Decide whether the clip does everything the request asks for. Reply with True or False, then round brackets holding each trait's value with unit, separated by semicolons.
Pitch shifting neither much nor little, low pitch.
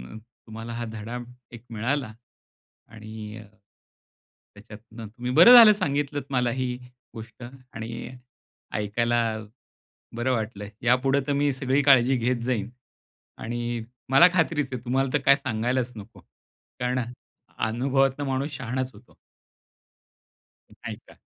True (3.1 semitones; 125 Hz)